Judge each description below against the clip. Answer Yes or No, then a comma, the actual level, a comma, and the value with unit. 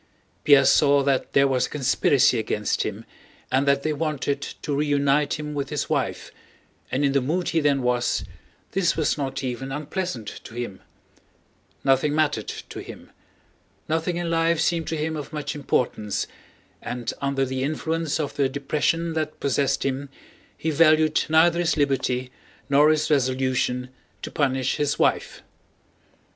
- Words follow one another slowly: No, average, 155 wpm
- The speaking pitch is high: No, medium, 140 Hz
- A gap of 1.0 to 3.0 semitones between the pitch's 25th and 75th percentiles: Yes, average, 2.7 semitones